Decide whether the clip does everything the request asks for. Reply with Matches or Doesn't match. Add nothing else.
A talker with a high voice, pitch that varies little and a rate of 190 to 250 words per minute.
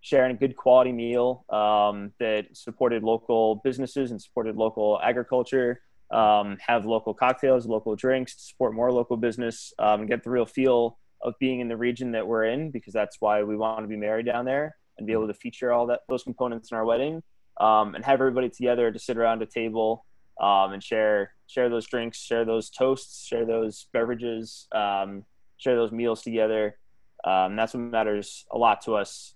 Doesn't match